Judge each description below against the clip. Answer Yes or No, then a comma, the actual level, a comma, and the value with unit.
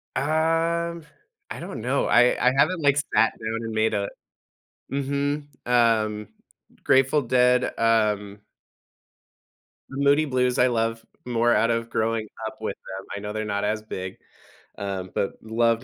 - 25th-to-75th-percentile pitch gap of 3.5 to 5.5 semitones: Yes, average, 3.9 semitones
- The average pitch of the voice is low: Yes, low, 115 Hz